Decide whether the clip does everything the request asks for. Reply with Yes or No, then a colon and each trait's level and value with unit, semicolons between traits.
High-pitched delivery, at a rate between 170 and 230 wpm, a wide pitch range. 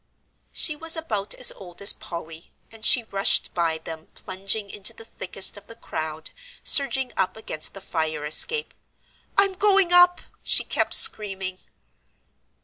No: high, 200 Hz; average, 145 wpm; wide, 8.2 semitones